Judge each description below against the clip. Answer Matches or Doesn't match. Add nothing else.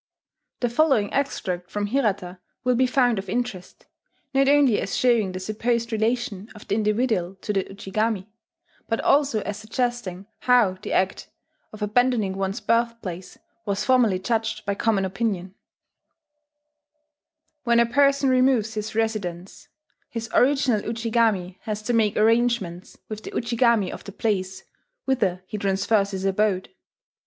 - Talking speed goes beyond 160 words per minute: Doesn't match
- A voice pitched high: Matches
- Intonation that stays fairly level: Doesn't match